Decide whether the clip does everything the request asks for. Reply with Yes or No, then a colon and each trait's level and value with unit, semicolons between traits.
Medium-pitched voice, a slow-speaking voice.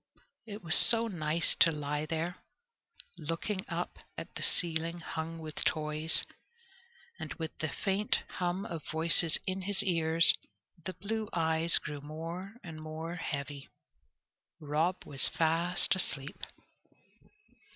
Yes: medium, 165 Hz; slow, 125 wpm